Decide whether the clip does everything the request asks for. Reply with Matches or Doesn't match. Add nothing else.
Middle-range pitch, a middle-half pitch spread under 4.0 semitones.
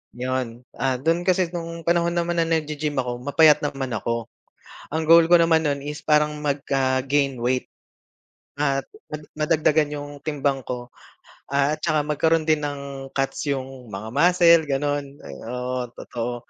Matches